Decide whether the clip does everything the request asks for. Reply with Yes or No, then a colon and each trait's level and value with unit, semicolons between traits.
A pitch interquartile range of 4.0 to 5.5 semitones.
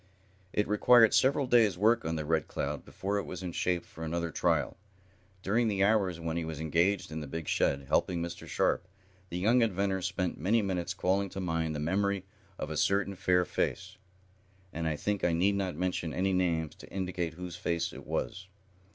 No: average, 3.1 semitones